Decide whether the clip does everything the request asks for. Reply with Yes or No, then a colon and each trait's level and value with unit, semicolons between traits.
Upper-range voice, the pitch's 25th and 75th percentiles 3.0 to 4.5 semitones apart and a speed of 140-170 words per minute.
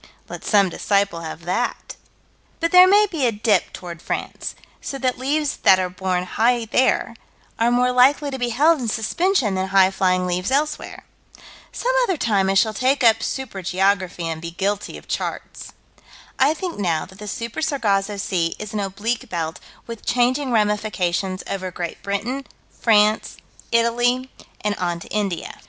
No: high, 210 Hz; average, 5.1 semitones; average, 165 wpm